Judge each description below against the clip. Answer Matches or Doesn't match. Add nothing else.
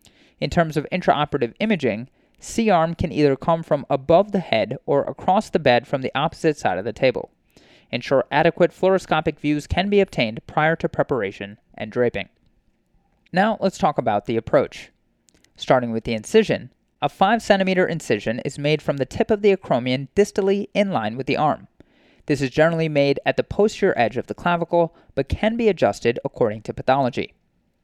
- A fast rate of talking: Doesn't match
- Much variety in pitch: Matches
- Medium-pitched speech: Matches